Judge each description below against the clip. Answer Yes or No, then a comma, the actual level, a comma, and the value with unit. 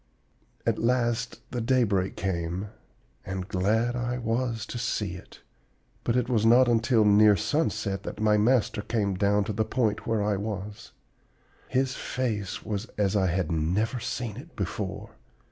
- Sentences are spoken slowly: No, average, 155 wpm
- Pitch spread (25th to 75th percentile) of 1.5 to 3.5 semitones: Yes, average, 3.1 semitones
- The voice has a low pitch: Yes, low, 105 Hz